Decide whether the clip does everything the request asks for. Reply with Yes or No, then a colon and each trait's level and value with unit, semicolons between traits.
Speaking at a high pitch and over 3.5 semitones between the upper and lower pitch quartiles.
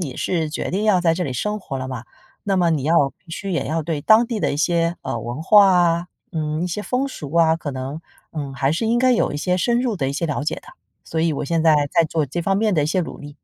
No: medium, 165 Hz; average, 4.3 semitones